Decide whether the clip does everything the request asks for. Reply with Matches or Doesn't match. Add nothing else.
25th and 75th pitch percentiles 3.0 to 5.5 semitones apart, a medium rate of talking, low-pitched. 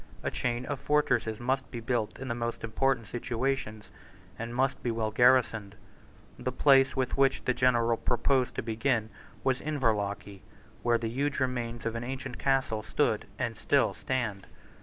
Doesn't match